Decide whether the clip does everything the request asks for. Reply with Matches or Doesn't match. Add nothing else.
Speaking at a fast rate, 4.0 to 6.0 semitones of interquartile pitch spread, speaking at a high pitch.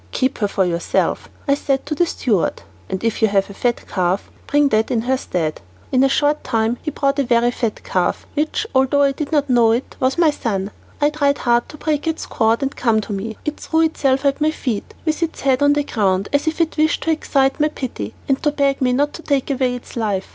Matches